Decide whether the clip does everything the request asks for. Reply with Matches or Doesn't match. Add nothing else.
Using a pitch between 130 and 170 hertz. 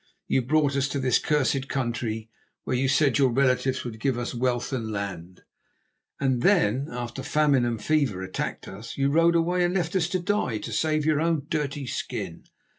Matches